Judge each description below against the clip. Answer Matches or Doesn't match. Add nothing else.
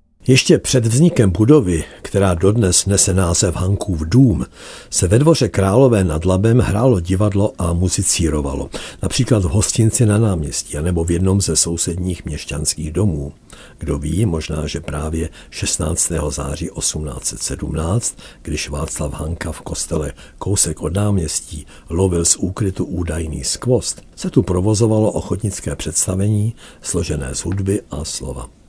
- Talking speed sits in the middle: Matches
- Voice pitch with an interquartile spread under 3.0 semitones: Doesn't match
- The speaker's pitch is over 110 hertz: Doesn't match